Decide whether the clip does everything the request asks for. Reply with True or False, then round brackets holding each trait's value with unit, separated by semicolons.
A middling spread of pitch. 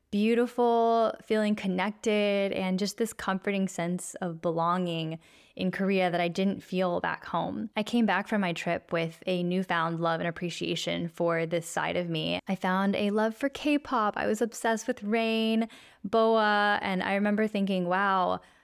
True (3.7 semitones)